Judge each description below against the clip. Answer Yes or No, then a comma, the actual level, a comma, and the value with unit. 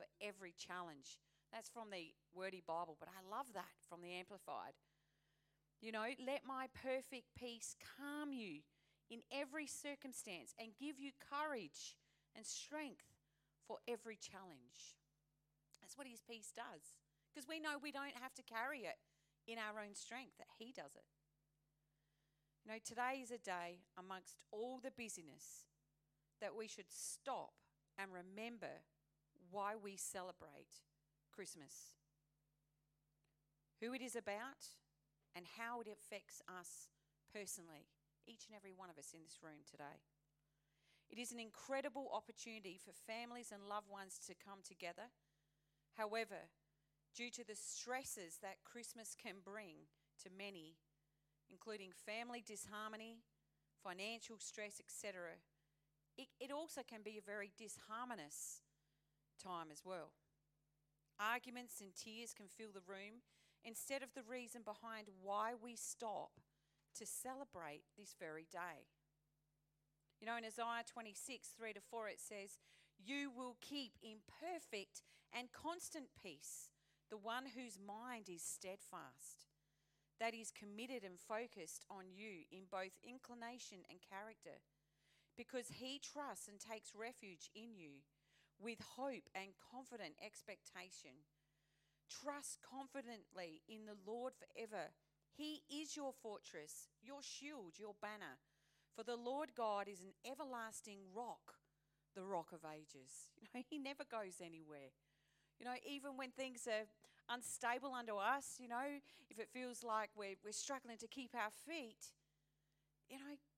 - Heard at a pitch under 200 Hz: No, high, 205 Hz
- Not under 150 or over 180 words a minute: No, average, 140 wpm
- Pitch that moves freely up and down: Yes, wide, 7.3 semitones